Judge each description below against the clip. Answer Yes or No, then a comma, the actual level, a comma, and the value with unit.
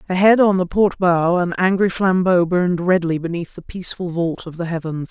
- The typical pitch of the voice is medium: Yes, medium, 175 Hz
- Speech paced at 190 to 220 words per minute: Yes, average, 200 wpm